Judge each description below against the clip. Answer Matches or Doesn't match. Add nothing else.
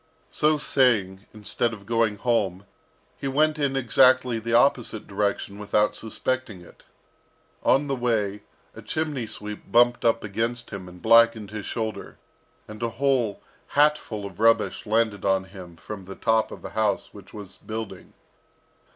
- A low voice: Matches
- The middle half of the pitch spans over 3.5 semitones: Doesn't match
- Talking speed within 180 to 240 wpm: Doesn't match